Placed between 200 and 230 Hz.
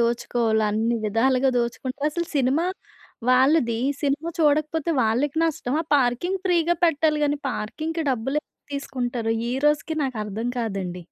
No: very high, 265 Hz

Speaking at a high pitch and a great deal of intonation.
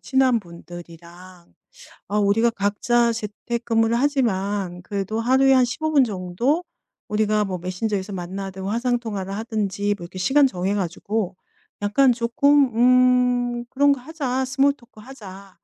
No: high, 215 Hz; average, 4.6 semitones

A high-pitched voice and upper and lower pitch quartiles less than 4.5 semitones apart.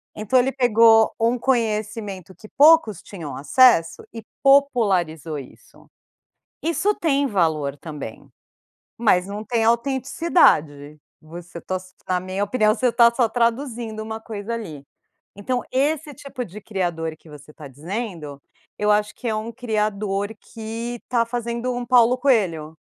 No: high, 220 Hz; average, 5.2 semitones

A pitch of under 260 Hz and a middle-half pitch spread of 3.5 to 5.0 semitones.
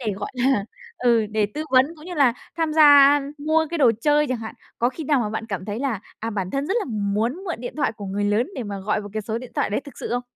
No: high, 240 Hz; wide, 5.5 semitones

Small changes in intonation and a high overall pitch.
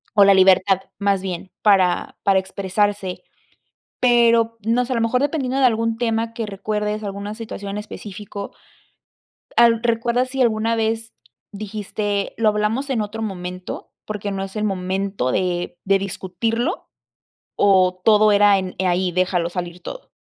No: average, 3.0 semitones; high, 205 Hz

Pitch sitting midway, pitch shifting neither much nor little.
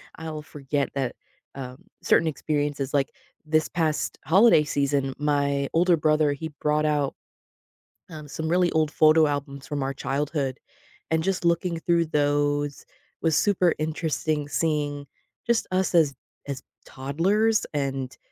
No: medium, 150 Hz; narrow, 2.3 semitones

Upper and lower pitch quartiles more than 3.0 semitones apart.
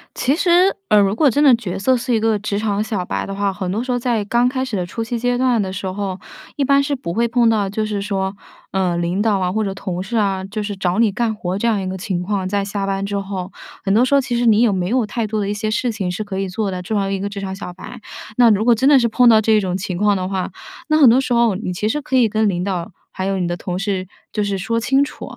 Yes: average, 3.5 semitones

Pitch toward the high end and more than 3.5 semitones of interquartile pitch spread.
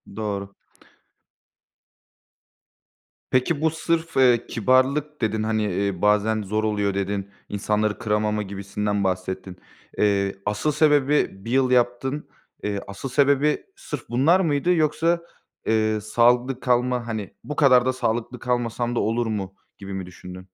No: low, 115 Hz; average, 4.5 semitones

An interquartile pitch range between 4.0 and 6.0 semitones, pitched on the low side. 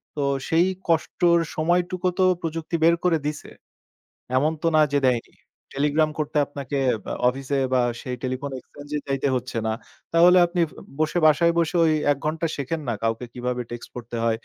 No: average, 4.3 semitones; medium, 150 Hz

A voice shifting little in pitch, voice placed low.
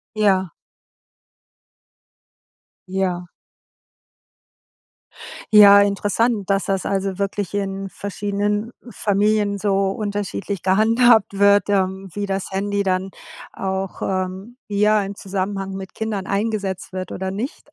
No: narrow, 1.2 semitones; high, 200 Hz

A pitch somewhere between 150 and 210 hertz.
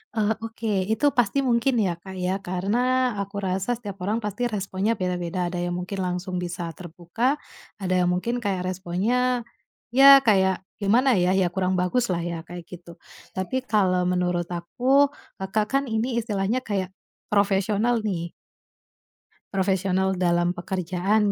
Yes: high, 190 Hz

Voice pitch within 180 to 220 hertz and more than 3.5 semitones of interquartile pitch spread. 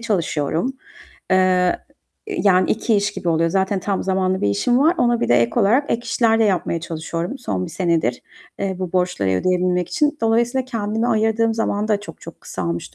Yes: high, 195 Hz; average, 4.8 semitones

